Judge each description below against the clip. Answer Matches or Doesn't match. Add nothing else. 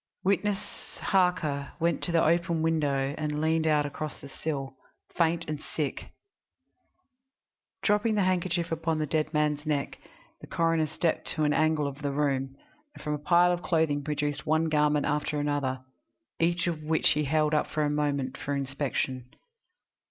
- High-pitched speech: Doesn't match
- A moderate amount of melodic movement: Doesn't match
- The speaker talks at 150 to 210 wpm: Matches